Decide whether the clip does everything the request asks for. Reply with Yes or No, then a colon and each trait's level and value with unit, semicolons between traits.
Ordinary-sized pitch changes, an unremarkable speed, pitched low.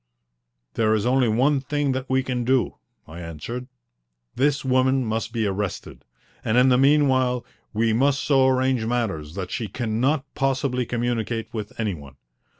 Yes: average, 3.1 semitones; average, 155 wpm; low, 125 Hz